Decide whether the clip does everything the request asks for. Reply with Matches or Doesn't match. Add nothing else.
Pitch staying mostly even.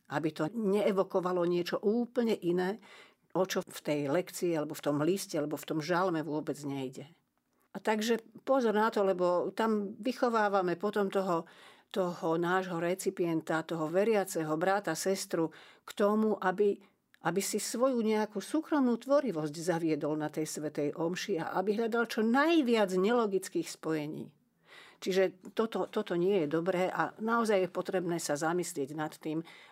Doesn't match